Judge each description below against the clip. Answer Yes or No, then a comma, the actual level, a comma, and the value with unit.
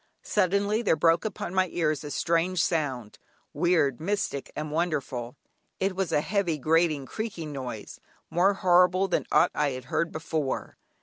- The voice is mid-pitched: Yes, medium, 165 Hz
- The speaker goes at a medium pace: Yes, average, 145 wpm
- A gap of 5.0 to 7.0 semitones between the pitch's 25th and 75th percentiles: No, average, 3.8 semitones